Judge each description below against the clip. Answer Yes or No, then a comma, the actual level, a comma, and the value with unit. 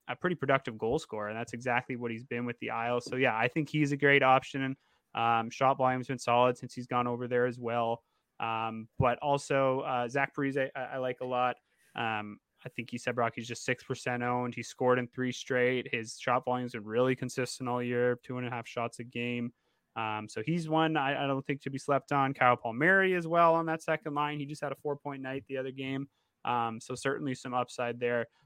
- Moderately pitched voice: No, low, 125 Hz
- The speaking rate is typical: No, fast, 235 wpm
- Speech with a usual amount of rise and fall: No, narrow, 2.2 semitones